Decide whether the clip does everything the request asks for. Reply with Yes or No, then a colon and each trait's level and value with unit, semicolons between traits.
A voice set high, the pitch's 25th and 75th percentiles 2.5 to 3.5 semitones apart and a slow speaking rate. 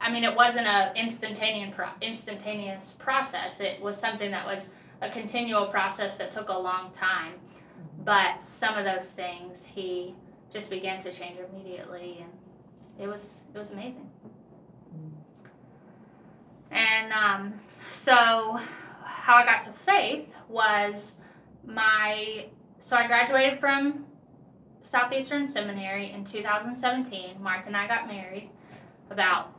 Yes: high, 205 Hz; average, 3.2 semitones; slow, 130 wpm